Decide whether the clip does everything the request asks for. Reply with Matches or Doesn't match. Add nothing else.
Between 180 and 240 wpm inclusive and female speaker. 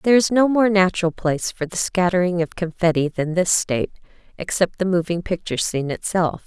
Matches